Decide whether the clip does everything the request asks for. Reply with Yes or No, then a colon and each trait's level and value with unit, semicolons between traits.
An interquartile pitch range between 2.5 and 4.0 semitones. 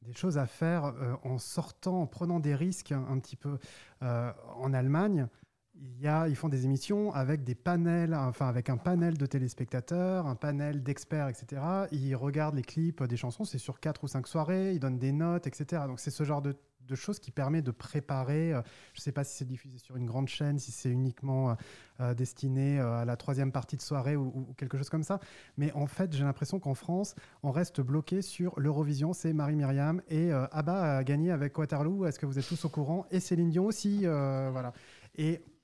Yes: average, 3.6 semitones